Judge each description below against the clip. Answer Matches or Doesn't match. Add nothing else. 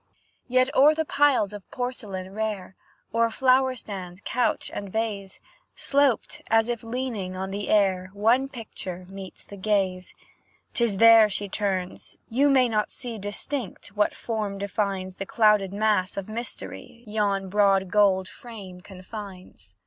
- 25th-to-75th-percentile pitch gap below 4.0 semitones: Matches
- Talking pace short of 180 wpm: Matches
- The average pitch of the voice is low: Doesn't match